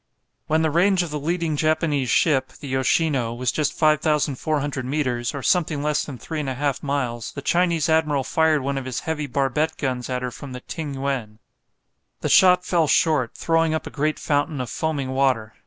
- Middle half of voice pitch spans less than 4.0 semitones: Yes, average, 3.2 semitones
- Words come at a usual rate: Yes, average, 190 wpm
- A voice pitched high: No, medium, 145 Hz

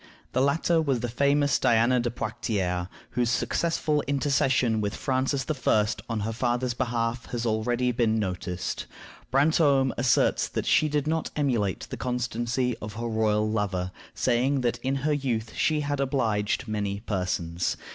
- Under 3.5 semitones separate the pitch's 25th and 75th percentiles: No, average, 3.8 semitones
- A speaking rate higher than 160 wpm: No, average, 150 wpm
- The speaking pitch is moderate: No, low, 120 Hz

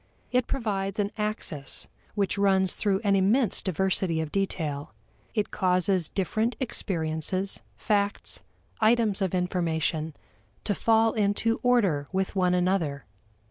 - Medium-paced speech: No, slow, 120 wpm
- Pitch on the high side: Yes, high, 195 Hz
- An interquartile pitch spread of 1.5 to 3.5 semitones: Yes, average, 3.1 semitones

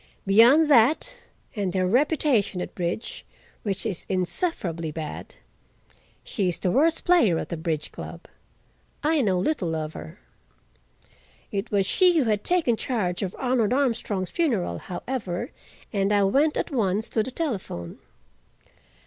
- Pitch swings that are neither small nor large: No, wide, 6.9 semitones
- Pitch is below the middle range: No, high, 210 Hz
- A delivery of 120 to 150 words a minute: Yes, slow, 135 wpm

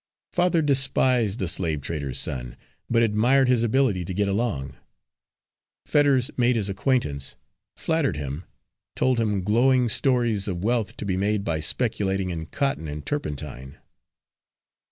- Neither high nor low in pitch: No, low, 105 Hz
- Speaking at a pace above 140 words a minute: No, slow, 135 wpm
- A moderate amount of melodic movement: No, wide, 7.3 semitones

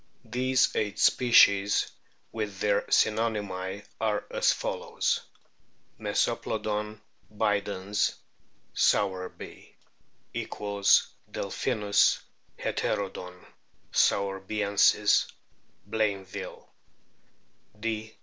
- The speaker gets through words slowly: Yes, slow, 65 wpm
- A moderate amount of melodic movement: No, narrow, 1.5 semitones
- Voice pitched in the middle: No, low, 105 Hz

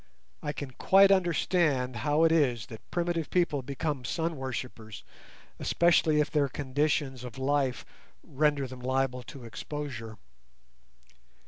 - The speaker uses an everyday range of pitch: Yes, average, 3.6 semitones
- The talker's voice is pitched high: No, medium, 140 Hz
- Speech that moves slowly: Yes, slow, 125 wpm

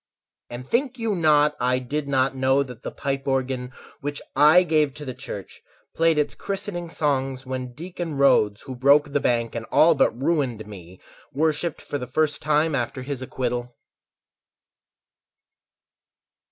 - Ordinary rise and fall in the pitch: Yes, average, 3.3 semitones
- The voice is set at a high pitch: No, medium, 140 Hz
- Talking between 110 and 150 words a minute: Yes, average, 145 wpm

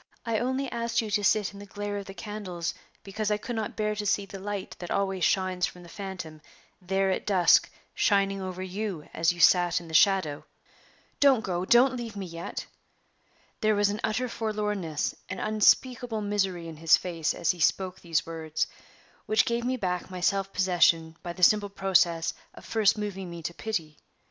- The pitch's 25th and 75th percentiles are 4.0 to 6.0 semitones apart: No, average, 3.3 semitones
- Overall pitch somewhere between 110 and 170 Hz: No, high, 195 Hz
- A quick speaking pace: No, average, 195 wpm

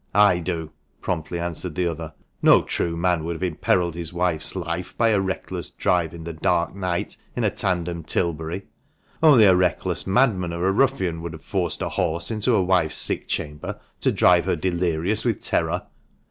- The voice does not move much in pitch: Yes, narrow, 2.1 semitones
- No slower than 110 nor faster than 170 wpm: No, average, 185 wpm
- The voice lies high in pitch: No, very low, 85 Hz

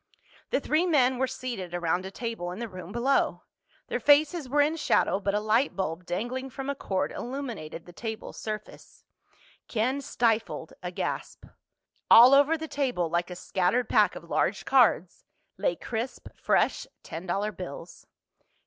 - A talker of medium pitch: No, high, 230 Hz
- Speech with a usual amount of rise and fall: No, wide, 6.5 semitones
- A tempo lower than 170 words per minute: Yes, average, 160 wpm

